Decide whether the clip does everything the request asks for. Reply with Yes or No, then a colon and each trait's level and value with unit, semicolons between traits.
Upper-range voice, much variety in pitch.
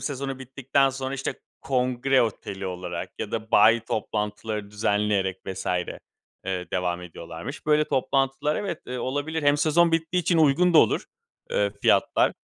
No: low, 130 Hz; wide, 6.0 semitones